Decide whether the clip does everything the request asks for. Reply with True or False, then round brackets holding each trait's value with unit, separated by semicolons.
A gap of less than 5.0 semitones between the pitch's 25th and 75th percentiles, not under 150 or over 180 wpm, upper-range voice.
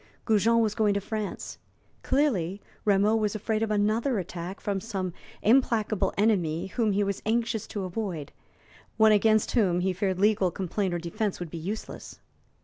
True (2.7 semitones; 160 wpm; 205 Hz)